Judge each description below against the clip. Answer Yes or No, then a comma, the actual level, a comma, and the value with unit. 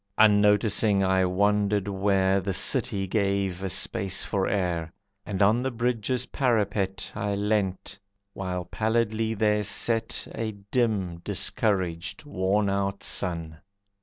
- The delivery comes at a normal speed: No, slow, 120 wpm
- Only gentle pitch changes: Yes, narrow, 2.3 semitones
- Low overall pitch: Yes, low, 100 Hz